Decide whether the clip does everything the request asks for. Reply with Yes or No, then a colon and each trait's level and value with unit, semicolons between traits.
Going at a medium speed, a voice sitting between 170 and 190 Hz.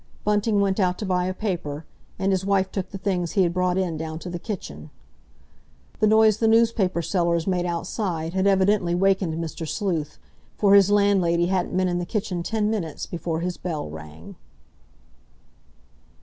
Yes: average, 175 wpm; medium, 185 Hz